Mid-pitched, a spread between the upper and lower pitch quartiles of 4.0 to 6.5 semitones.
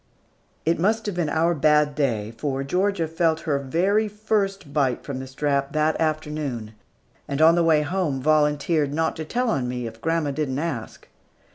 No: medium, 155 Hz; average, 3.3 semitones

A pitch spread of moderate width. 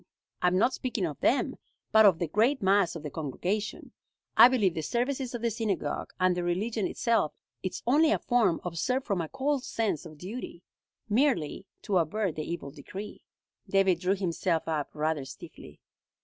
No: wide, 5.8 semitones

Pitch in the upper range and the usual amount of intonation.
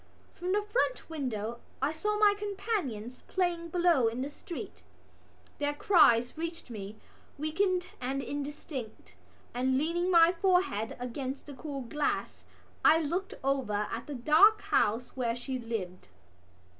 No: very high, 290 Hz; wide, 6.4 semitones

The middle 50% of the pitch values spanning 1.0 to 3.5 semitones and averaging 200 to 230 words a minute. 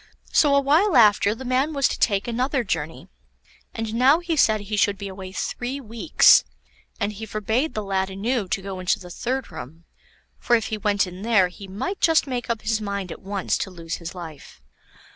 No: average, 4.7 semitones; fast, 205 wpm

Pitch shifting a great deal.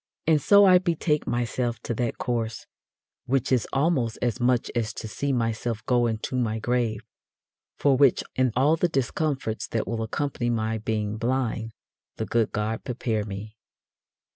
No: average, 3.2 semitones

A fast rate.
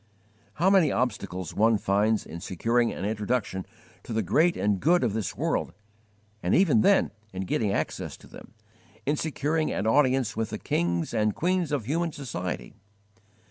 No: average, 165 wpm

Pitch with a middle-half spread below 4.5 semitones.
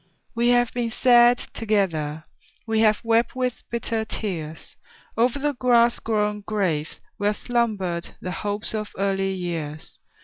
Yes: average, 3.8 semitones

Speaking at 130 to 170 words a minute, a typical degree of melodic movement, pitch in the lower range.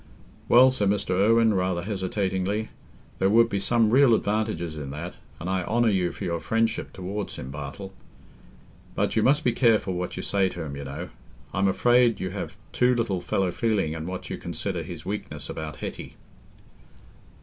No: average, 180 wpm; average, 4.2 semitones; very low, 95 Hz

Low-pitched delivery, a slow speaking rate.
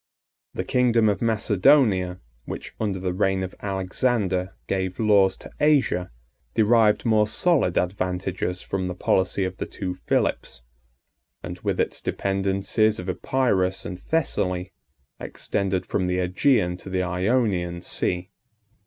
Yes: very low, 95 Hz; slow, 130 wpm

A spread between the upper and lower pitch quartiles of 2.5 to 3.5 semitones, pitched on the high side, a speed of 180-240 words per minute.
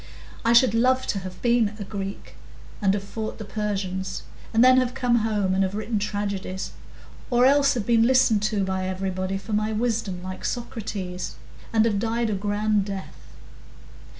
No: average, 3.2 semitones; high, 210 Hz; average, 170 wpm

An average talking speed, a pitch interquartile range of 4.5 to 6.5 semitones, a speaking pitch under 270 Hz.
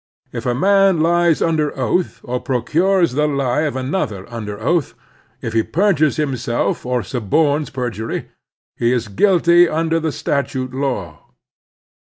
Yes: average, 145 wpm; average, 5.3 semitones; medium, 140 Hz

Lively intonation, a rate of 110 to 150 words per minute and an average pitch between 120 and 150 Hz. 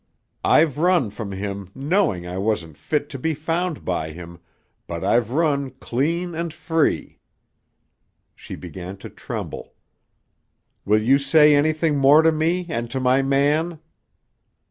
Yes: wide, 7.6 semitones; average, 140 wpm; medium, 140 Hz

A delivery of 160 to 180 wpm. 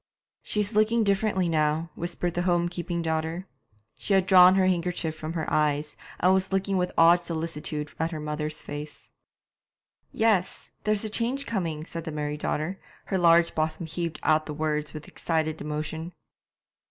Yes: average, 165 wpm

